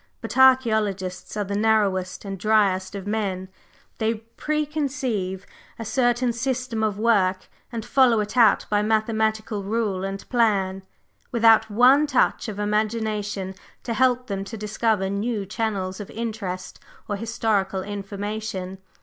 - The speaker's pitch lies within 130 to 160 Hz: No, high, 215 Hz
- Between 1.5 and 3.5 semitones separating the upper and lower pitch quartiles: Yes, average, 2.8 semitones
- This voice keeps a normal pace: No, slow, 130 wpm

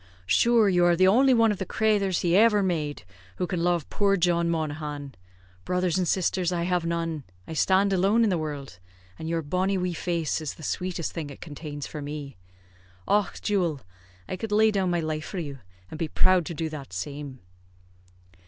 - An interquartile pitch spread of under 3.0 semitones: No, average, 3.6 semitones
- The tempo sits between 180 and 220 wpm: Yes, average, 195 wpm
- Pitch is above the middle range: No, medium, 175 Hz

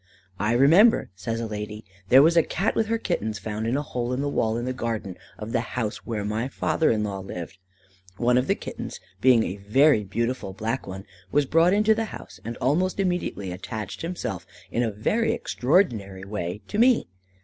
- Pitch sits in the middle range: No, low, 115 Hz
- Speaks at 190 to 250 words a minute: Yes, average, 200 wpm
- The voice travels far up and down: Yes, wide, 6.3 semitones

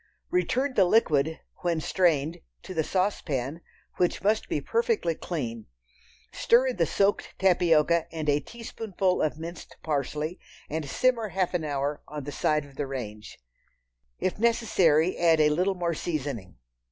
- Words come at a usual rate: Yes, average, 150 wpm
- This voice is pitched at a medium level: Yes, medium, 165 Hz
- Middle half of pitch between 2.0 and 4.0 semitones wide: No, average, 4.5 semitones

